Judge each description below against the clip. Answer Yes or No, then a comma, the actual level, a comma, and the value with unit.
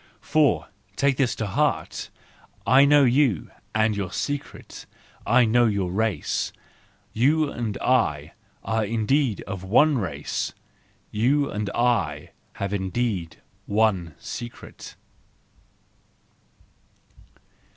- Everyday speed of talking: No, slow, 100 wpm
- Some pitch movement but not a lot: Yes, average, 4.8 semitones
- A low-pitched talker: Yes, low, 110 Hz